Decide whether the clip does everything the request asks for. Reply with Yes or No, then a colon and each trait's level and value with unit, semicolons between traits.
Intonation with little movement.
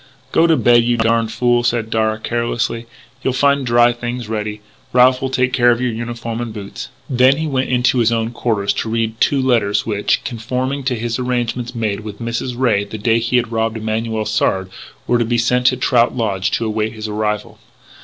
Yes: narrow, 2.0 semitones